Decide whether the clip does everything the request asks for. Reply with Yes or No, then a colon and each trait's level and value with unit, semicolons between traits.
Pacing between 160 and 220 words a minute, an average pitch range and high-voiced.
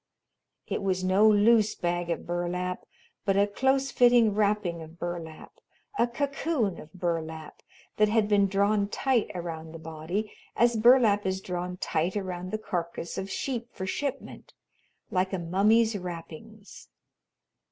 No: average, 140 wpm; average, 3.8 semitones; high, 195 Hz